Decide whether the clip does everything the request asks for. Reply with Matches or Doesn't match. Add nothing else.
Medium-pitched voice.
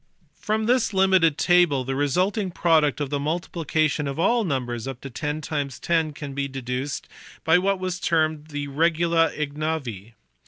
Matches